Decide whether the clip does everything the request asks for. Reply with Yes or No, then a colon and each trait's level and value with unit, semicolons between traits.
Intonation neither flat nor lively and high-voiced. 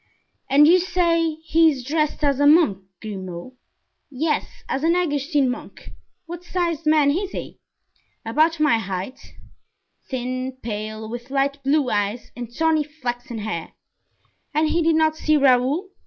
Yes: average, 4.7 semitones; very high, 285 Hz